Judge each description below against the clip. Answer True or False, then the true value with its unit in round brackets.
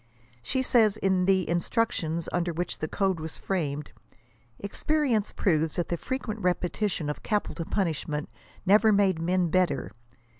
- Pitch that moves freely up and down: False (4.1 semitones)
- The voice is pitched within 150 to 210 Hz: True (185 Hz)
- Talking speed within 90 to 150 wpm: True (140 wpm)